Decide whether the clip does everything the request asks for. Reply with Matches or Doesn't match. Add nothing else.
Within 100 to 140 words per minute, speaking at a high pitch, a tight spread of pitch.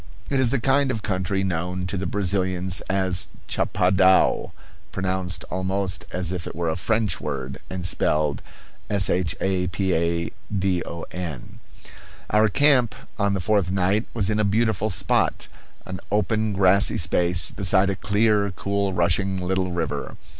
Doesn't match